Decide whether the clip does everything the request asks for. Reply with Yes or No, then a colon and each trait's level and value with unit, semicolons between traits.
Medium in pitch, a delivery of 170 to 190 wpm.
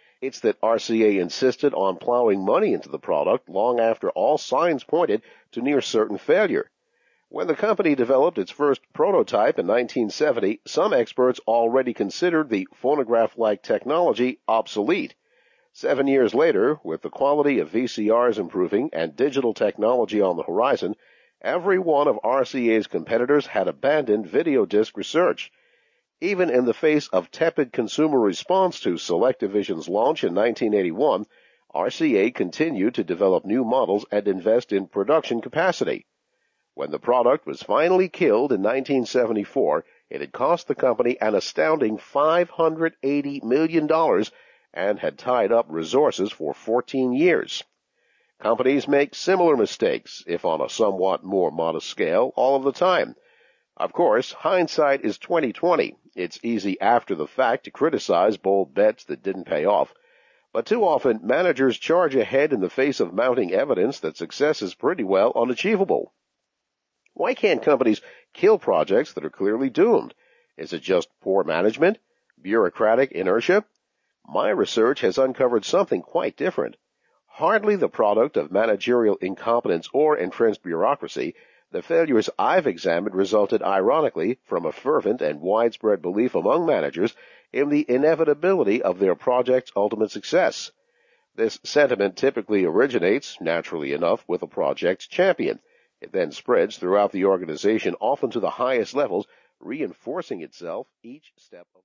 No: medium, 155 Hz; average, 145 wpm